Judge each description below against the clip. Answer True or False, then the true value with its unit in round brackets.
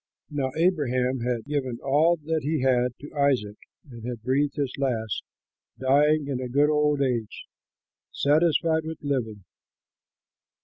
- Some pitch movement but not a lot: True (3.0 semitones)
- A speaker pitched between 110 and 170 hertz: True (140 Hz)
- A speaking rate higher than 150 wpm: False (135 wpm)